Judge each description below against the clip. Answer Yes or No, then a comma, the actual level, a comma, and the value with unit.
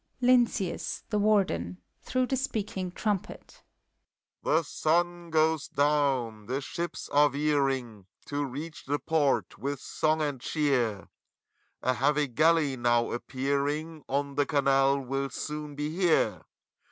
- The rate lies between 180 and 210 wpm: No, slow, 135 wpm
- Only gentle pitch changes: No, average, 3.3 semitones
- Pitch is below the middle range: No, medium, 145 Hz